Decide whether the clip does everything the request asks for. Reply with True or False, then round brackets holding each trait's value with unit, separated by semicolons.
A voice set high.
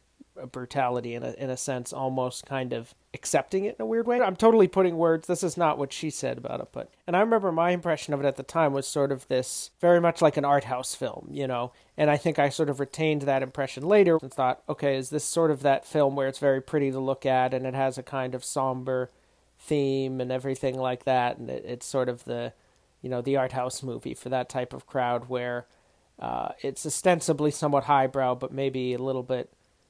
False (135 Hz)